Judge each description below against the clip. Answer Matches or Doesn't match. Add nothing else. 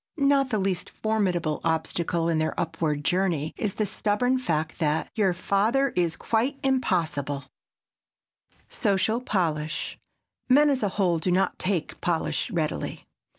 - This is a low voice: Doesn't match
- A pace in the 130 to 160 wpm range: Matches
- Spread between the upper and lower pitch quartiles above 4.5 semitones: Matches